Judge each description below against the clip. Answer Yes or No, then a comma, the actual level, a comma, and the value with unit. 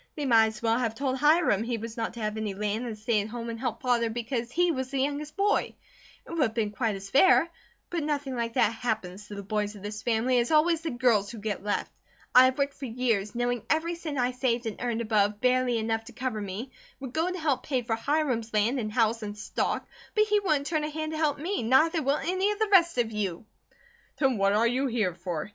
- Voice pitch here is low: No, high, 240 Hz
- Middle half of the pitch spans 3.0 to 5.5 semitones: Yes, average, 4.8 semitones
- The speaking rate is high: Yes, fast, 250 wpm